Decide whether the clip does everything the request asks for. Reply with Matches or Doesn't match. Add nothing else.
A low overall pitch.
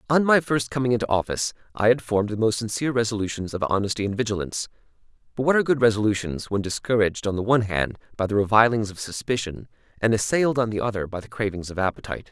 Matches